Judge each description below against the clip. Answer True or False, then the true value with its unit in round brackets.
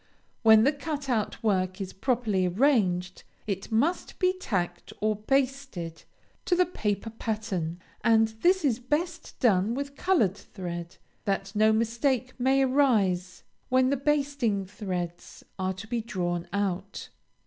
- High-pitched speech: True (220 Hz)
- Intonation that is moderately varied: False (6.2 semitones)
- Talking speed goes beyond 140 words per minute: False (135 wpm)